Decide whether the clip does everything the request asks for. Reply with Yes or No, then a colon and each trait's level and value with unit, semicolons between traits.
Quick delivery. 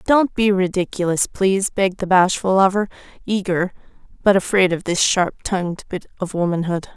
No: average, 155 wpm